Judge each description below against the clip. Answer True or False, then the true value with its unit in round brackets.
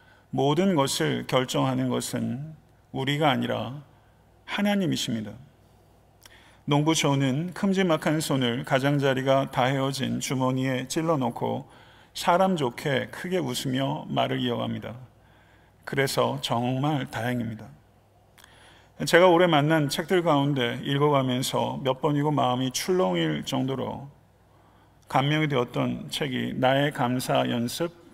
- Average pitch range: True (3.5 semitones)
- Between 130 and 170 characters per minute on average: False (255 characters per minute)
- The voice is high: False (130 Hz)